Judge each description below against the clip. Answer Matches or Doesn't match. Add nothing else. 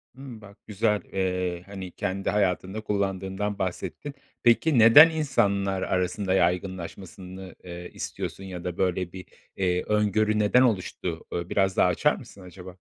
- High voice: Doesn't match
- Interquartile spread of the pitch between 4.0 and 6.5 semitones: Doesn't match